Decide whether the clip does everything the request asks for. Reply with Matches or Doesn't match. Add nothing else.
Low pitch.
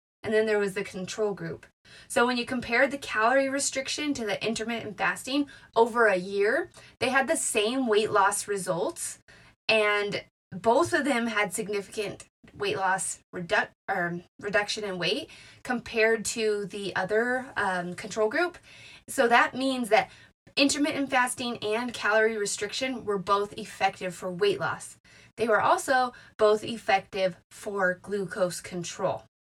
Doesn't match